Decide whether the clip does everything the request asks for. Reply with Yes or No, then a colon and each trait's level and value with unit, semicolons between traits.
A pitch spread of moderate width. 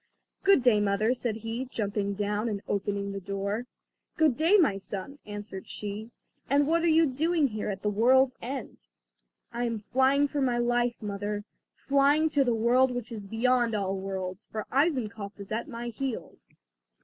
Yes: average, 4.4 semitones